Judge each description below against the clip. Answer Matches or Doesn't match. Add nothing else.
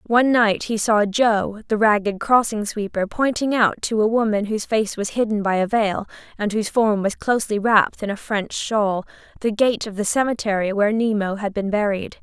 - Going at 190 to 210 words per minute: Matches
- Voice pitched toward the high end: Matches